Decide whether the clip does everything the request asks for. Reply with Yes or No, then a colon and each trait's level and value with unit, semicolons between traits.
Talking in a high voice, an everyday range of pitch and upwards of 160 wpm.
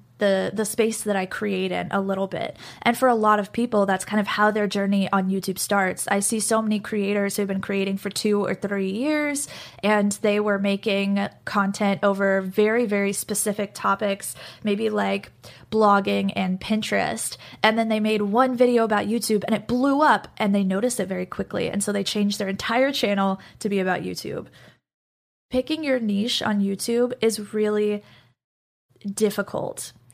No: high, 205 Hz; narrow, 1.7 semitones; average, 180 wpm